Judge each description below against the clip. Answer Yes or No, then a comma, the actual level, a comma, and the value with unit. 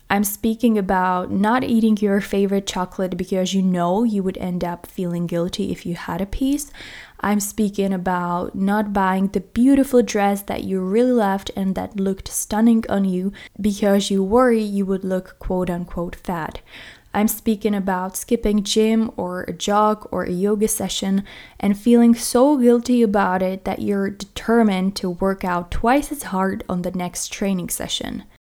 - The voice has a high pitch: Yes, high, 200 Hz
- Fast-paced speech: No, average, 170 wpm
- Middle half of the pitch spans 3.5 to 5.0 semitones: No, average, 2.8 semitones